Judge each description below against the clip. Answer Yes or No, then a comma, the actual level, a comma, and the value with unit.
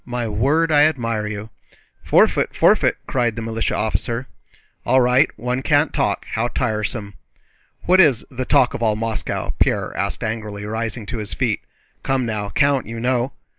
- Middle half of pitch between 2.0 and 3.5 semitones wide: Yes, average, 3.1 semitones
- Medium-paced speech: Yes, average, 160 wpm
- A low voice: Yes, low, 115 Hz